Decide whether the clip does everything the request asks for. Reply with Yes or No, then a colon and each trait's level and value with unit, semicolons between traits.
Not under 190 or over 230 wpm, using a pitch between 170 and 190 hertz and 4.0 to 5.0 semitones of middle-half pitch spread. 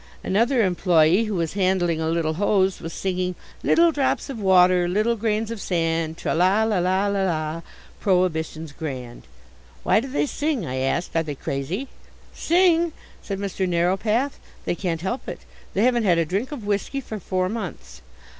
No: average, 175 wpm; medium, 185 Hz; average, 4.7 semitones